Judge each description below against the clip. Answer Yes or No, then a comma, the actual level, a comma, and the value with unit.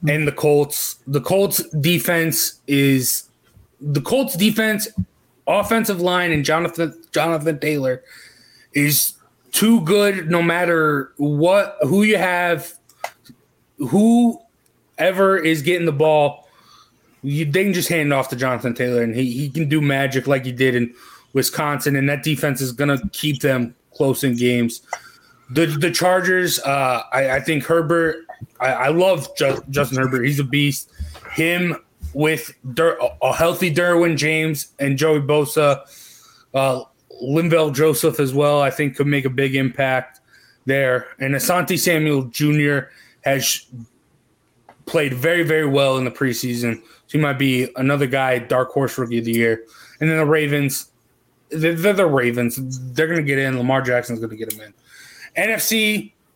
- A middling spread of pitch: Yes, average, 3.9 semitones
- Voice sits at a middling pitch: Yes, medium, 145 Hz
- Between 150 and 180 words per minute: Yes, average, 155 wpm